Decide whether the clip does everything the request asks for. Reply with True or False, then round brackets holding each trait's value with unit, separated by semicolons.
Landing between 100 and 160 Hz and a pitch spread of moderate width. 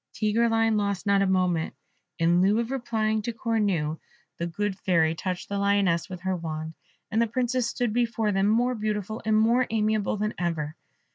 False (210 Hz; 3.6 semitones)